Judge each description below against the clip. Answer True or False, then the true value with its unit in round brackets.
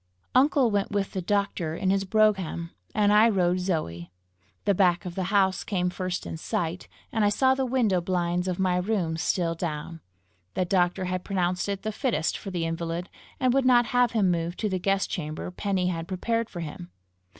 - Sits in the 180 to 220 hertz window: True (185 Hz)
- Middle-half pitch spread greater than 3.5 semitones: False (2.9 semitones)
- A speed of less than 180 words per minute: False (195 wpm)